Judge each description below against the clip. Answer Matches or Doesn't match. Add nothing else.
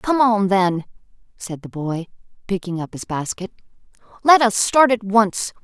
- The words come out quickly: Doesn't match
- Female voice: Matches